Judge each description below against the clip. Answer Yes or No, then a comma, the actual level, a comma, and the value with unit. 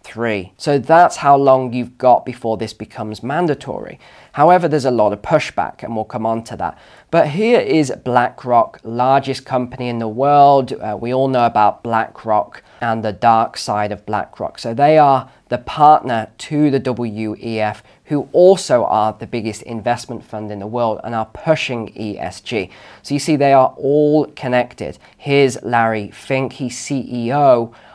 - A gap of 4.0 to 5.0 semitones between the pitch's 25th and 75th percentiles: No, average, 3.6 semitones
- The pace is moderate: Yes, average, 165 wpm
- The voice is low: Yes, low, 120 Hz